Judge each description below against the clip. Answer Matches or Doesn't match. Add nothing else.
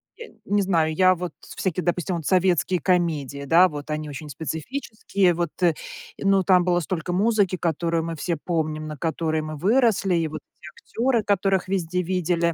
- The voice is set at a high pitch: Doesn't match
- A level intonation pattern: Doesn't match